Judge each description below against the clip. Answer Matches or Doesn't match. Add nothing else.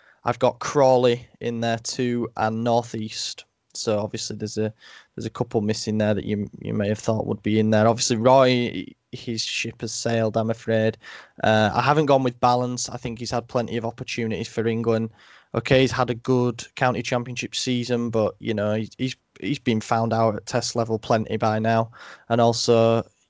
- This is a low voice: Matches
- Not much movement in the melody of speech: Matches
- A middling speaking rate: Matches